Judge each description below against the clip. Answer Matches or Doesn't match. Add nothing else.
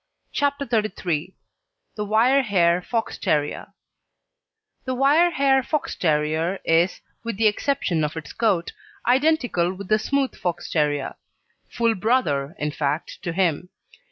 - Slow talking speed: Matches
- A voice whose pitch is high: Matches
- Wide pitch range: Matches